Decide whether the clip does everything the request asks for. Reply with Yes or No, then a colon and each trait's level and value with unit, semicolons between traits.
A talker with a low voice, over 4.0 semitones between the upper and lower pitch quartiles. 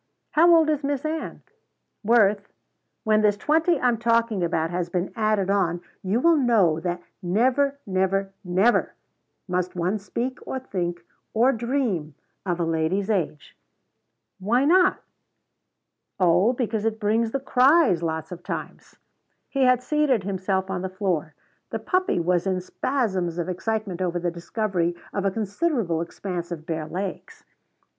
No: high, 200 Hz; wide, 5.4 semitones